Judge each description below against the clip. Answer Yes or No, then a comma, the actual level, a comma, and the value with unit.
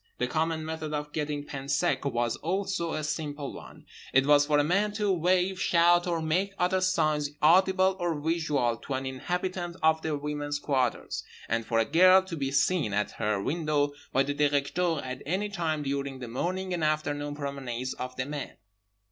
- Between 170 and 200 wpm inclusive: Yes, average, 180 wpm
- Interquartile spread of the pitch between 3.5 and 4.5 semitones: Yes, average, 3.9 semitones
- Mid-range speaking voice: Yes, medium, 150 Hz